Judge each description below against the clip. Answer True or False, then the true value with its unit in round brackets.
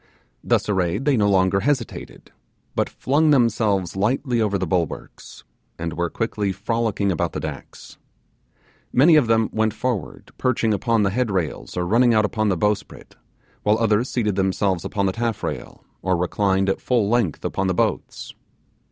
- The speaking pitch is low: True (105 Hz)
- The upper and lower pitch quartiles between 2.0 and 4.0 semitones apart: True (3.5 semitones)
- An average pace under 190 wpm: True (160 wpm)